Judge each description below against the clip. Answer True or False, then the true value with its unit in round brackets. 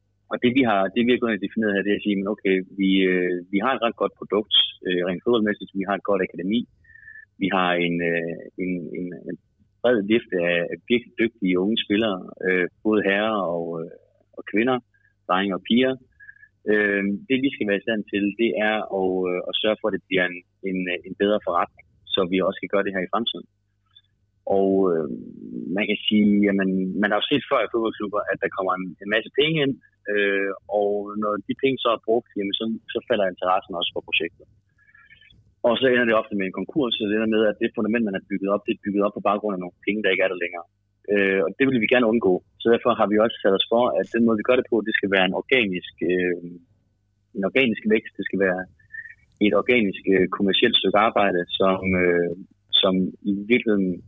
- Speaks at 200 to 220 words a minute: True (210 wpm)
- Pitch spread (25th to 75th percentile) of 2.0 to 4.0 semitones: True (2.8 semitones)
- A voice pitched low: True (100 Hz)